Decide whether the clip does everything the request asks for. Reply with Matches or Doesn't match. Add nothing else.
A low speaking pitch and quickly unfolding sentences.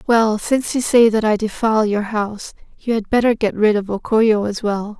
Doesn't match